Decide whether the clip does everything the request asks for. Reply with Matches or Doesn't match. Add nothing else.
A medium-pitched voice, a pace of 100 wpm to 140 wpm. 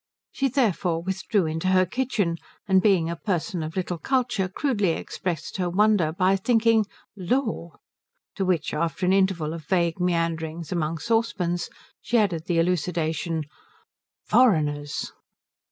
Matches